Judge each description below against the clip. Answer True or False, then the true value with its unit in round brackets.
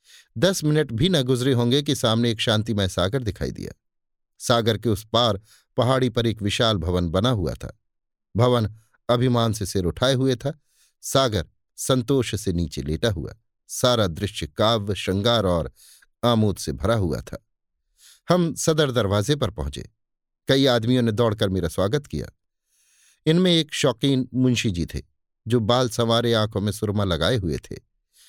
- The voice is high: False (115 Hz)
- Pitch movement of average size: True (4.1 semitones)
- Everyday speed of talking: True (160 wpm)